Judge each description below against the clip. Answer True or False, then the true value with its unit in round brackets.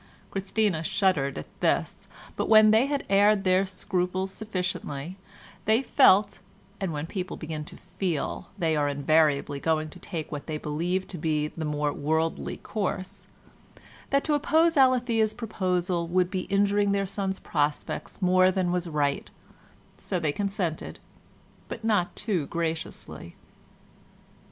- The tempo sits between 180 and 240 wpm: False (140 wpm)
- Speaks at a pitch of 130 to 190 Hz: True (185 Hz)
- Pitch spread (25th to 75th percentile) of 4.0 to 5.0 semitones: True (4.3 semitones)